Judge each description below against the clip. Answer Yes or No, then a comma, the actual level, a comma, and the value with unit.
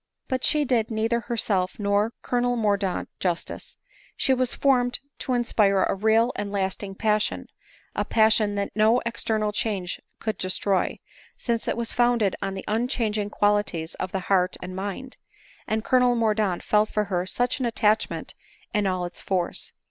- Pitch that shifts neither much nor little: Yes, average, 3.2 semitones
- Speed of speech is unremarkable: Yes, average, 170 wpm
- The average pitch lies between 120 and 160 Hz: No, high, 215 Hz